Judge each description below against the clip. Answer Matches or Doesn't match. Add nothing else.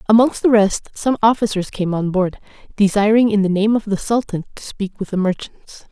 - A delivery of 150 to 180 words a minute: Doesn't match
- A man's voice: Doesn't match